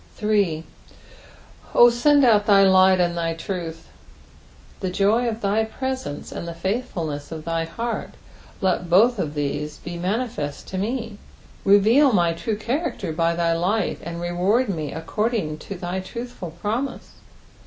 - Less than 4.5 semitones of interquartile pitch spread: No, average, 5.0 semitones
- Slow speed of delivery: No, average, 145 wpm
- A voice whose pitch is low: No, high, 190 Hz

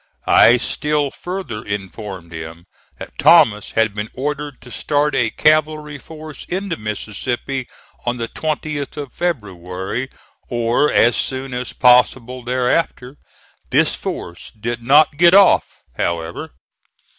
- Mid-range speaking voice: No, low, 125 Hz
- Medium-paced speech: No, slow, 120 wpm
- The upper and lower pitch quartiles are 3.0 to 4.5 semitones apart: No, wide, 5.6 semitones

